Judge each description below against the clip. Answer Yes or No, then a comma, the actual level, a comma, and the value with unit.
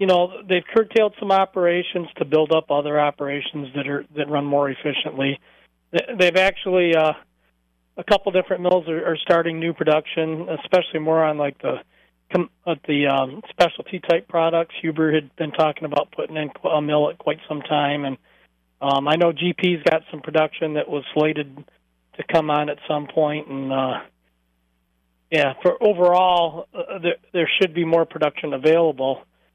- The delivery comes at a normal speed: Yes, average, 170 wpm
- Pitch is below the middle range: No, medium, 155 Hz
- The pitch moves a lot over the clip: No, average, 3.2 semitones